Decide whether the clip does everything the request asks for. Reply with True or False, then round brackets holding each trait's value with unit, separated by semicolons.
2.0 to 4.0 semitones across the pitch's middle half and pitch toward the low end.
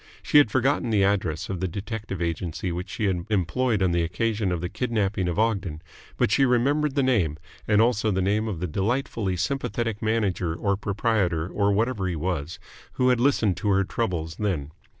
False (4.4 semitones; 100 Hz)